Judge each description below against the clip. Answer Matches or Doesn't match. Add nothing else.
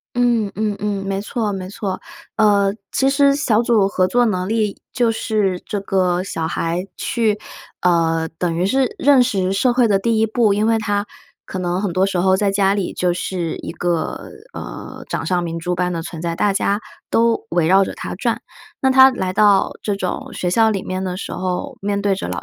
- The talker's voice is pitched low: Doesn't match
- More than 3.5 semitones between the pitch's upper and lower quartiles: Doesn't match